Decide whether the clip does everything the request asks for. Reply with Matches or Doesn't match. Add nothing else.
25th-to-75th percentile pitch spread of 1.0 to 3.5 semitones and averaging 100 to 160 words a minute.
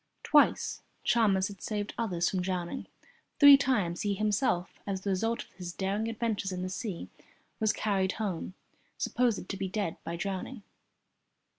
Matches